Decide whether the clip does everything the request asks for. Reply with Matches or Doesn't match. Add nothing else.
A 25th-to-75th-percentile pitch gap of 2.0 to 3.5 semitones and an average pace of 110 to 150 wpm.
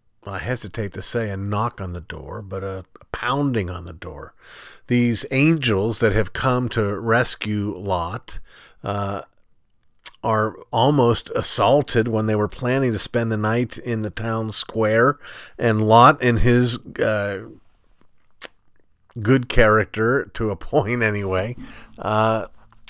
Matches